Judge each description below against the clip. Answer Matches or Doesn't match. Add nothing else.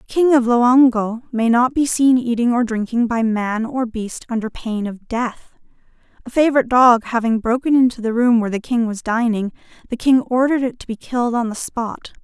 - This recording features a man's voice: Doesn't match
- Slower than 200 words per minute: Doesn't match